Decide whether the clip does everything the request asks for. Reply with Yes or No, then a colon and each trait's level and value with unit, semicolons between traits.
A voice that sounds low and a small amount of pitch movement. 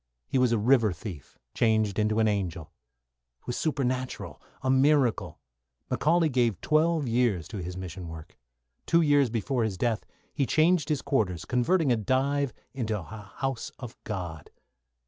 No: low, 120 Hz; average, 5.3 semitones